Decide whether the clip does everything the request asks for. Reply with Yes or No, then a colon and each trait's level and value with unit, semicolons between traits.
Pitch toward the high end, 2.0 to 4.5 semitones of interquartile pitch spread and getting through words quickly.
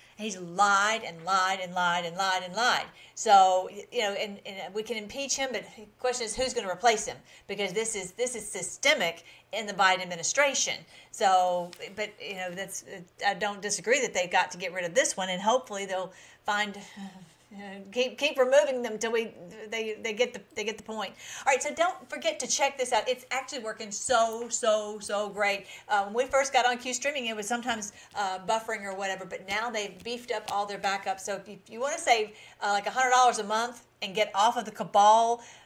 Yes: high, 215 Hz; average, 3.6 semitones; fast, 220 wpm